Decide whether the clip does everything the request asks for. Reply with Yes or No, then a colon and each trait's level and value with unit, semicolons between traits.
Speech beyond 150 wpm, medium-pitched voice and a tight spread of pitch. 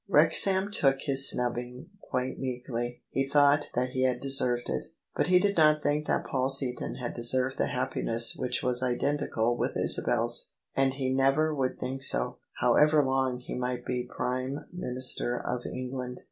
No: average, 165 wpm; low, 130 Hz; narrow, 1.9 semitones